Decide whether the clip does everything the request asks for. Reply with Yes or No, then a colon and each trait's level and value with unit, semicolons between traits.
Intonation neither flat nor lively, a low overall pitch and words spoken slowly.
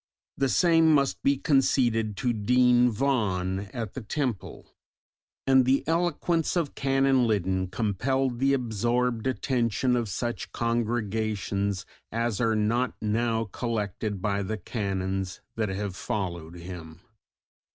Yes: average, 4.4 semitones; low, 115 Hz; slow, 120 wpm